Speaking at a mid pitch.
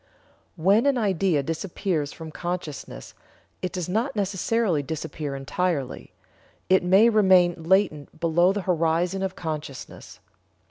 Yes: medium, 180 Hz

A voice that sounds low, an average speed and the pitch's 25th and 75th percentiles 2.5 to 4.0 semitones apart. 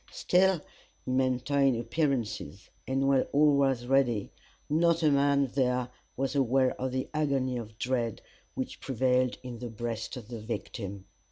Yes: low, 130 Hz; average, 150 wpm; average, 2.8 semitones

